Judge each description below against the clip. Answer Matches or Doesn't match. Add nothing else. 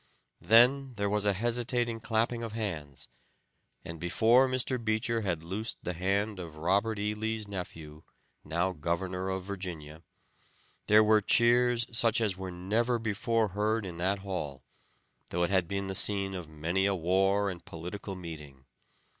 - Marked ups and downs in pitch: Doesn't match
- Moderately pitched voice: Doesn't match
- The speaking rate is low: Doesn't match